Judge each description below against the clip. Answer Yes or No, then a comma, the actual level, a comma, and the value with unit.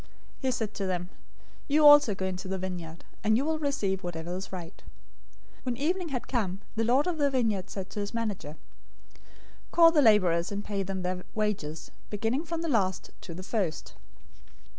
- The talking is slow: No, average, 185 wpm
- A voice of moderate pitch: No, high, 205 Hz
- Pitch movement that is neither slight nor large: No, wide, 6.0 semitones